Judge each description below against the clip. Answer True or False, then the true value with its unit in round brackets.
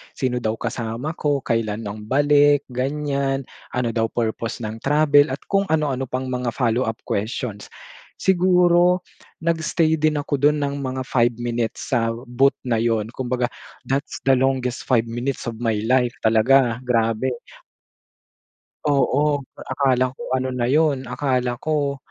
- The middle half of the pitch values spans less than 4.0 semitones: True (3.4 semitones)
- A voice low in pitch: True (130 Hz)